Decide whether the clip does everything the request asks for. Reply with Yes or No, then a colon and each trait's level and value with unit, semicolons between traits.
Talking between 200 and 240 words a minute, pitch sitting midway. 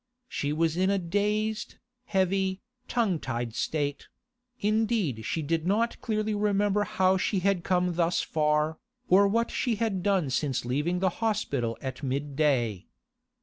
No: average, 145 wpm; medium, 180 Hz